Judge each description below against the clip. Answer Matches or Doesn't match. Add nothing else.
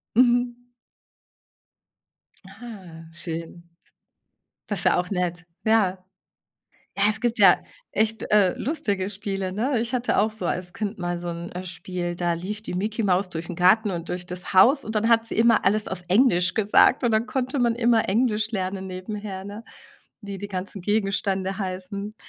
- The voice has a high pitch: Matches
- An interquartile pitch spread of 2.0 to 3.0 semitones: Doesn't match